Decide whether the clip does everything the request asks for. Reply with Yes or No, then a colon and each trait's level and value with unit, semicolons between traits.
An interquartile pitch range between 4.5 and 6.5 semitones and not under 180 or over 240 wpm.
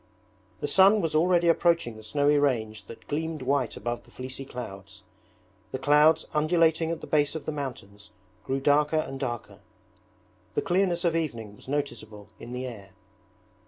No: average, 5.2 semitones; average, 160 wpm